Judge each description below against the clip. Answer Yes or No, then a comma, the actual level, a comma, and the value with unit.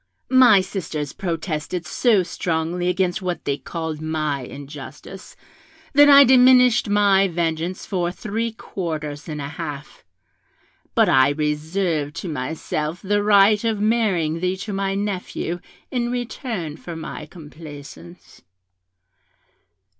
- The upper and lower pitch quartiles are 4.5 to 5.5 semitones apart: Yes, average, 4.8 semitones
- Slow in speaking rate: Yes, slow, 120 wpm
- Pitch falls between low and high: Yes, medium, 175 Hz